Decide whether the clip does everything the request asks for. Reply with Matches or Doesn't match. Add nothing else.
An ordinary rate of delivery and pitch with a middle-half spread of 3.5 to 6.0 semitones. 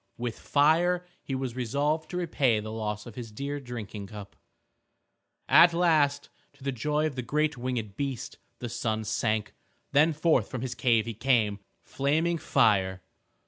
Matches